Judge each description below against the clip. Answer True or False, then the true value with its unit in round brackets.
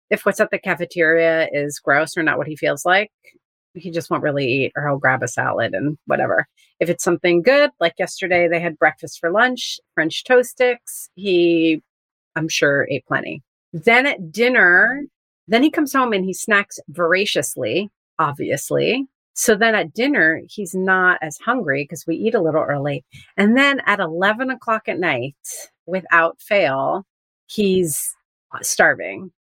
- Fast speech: False (165 wpm)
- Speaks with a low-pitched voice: False (180 Hz)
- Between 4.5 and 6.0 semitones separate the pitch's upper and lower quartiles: True (5.5 semitones)